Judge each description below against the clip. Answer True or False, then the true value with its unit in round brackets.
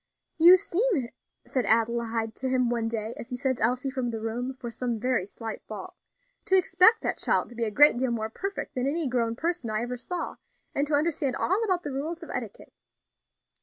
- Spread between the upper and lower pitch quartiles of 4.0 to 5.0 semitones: True (4.7 semitones)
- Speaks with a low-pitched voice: False (250 Hz)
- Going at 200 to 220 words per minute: True (205 wpm)